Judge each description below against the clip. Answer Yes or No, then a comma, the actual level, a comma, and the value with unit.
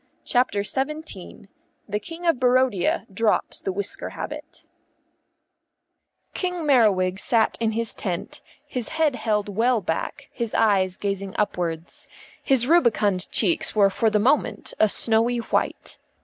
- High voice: Yes, high, 220 Hz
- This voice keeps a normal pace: No, slow, 130 wpm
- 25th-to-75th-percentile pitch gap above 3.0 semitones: Yes, average, 4.4 semitones